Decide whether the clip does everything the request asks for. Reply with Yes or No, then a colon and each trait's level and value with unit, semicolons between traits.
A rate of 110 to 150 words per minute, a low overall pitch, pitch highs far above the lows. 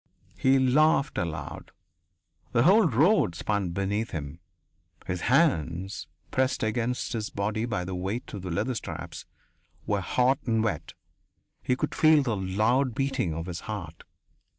Yes: average, 145 wpm; low, 110 Hz; wide, 6.2 semitones